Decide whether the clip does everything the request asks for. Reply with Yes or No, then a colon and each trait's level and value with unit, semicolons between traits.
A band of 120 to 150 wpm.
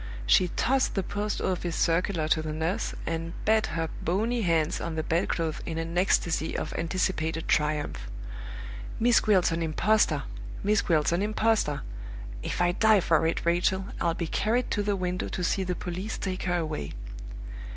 No: average, 170 wpm